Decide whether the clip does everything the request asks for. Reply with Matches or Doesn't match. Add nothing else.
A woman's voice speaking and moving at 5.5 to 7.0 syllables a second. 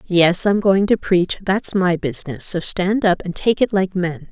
Doesn't match